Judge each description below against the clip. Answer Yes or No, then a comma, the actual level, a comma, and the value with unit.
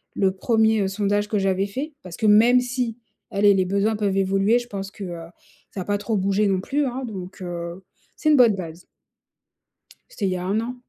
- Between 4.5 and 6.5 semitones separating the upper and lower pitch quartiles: No, average, 2.8 semitones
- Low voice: No, high, 200 Hz